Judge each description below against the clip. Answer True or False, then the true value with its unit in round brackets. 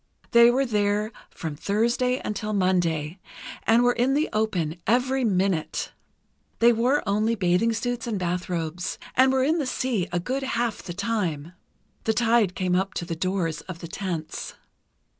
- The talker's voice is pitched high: True (205 Hz)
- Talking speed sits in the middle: True (160 wpm)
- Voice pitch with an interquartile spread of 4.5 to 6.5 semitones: True (5.1 semitones)